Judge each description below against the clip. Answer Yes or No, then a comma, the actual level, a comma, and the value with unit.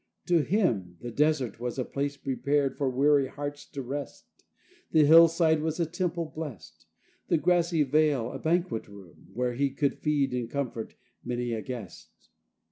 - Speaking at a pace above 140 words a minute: Yes, average, 160 wpm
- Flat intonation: No, average, 4.3 semitones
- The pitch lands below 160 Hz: Yes, medium, 140 Hz